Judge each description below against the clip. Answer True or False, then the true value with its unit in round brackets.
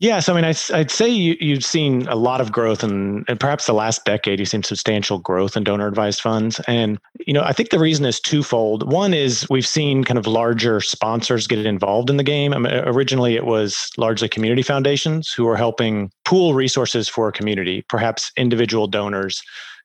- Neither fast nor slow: False (210 wpm)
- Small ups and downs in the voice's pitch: False (4.5 semitones)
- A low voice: True (115 Hz)